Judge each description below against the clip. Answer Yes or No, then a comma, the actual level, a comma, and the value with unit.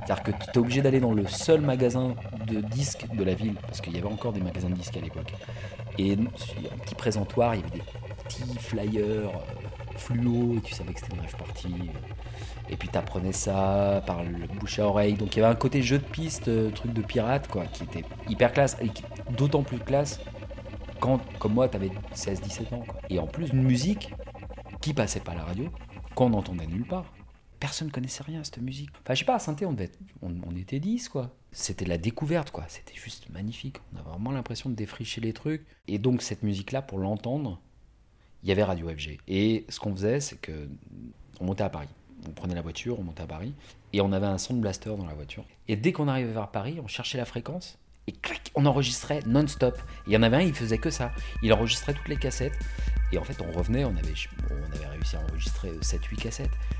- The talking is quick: Yes, fast, 235 wpm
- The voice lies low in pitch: Yes, low, 110 Hz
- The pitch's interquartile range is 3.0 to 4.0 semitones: No, average, 4.8 semitones